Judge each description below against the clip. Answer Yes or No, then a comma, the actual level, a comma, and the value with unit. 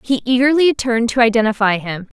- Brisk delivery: No, average, 165 wpm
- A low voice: No, high, 235 Hz